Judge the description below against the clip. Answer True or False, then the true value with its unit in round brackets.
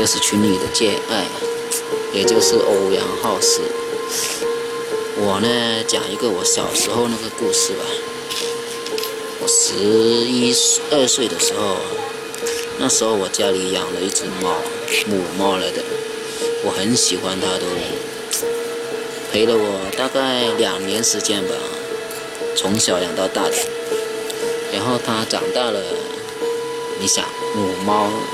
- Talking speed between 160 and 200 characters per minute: True (175 characters per minute)